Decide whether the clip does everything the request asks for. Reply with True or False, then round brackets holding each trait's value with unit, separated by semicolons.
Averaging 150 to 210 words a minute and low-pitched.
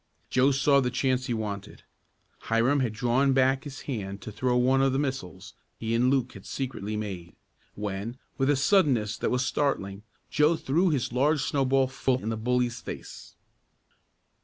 True (170 wpm; 125 Hz)